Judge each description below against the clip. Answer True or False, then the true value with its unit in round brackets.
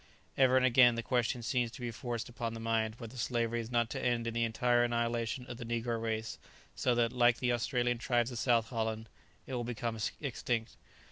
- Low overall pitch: True (120 Hz)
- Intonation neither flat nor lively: False (1.1 semitones)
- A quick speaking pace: True (210 wpm)